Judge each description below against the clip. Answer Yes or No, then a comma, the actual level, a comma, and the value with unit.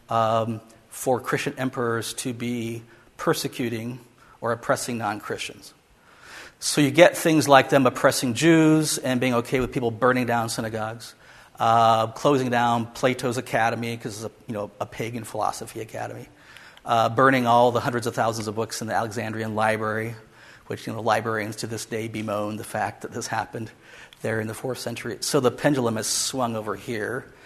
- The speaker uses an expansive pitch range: No, narrow, 2.4 semitones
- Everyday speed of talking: Yes, average, 175 wpm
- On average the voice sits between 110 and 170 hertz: Yes, low, 115 Hz